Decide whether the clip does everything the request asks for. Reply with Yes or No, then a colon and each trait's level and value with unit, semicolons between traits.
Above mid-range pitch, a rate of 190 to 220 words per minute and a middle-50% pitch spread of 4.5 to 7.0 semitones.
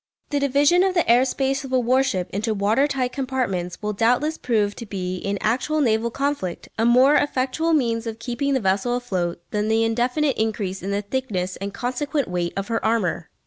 Yes: high, 235 Hz; average, 195 wpm; average, 4.9 semitones